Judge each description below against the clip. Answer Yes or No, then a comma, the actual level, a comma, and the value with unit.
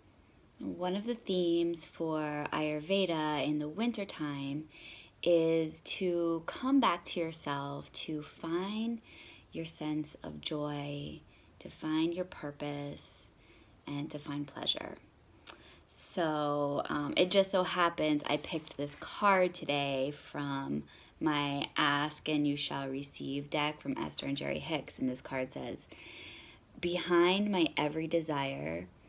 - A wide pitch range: No, average, 3.1 semitones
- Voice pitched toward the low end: No, medium, 150 Hz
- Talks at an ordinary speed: No, slow, 130 wpm